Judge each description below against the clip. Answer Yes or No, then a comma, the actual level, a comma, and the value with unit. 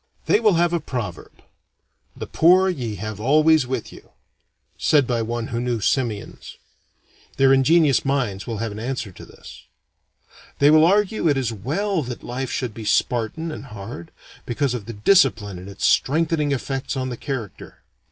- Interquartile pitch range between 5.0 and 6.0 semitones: Yes, wide, 5.4 semitones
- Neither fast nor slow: Yes, average, 170 wpm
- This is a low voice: Yes, low, 130 Hz